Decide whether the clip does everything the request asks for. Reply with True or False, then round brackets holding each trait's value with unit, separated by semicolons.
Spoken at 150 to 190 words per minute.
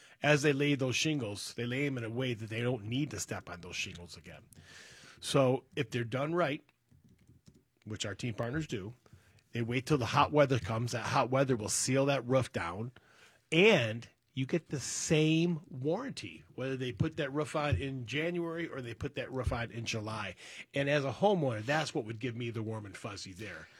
False (205 wpm)